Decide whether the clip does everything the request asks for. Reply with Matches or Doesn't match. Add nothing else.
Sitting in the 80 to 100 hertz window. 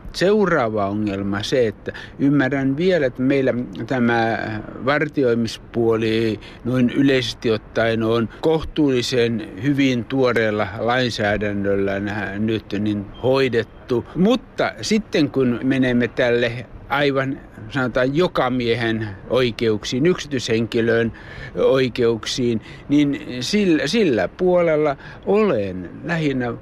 Doesn't match